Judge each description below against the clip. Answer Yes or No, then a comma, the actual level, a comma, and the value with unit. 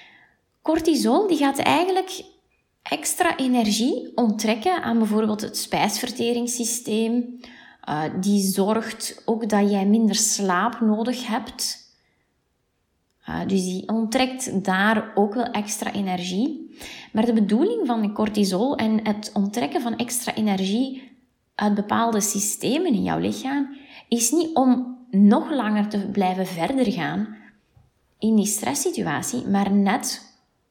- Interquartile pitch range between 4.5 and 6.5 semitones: No, average, 3.6 semitones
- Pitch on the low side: No, high, 230 Hz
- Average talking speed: No, slow, 120 wpm